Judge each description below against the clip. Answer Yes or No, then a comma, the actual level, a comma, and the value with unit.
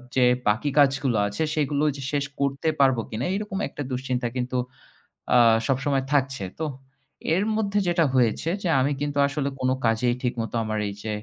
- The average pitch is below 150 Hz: Yes, low, 135 Hz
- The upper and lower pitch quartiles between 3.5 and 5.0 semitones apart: No, average, 2.9 semitones